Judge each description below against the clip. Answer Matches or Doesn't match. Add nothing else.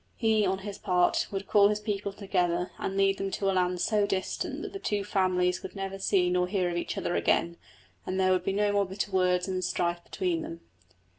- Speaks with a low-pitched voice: Doesn't match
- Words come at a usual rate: Doesn't match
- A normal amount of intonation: Doesn't match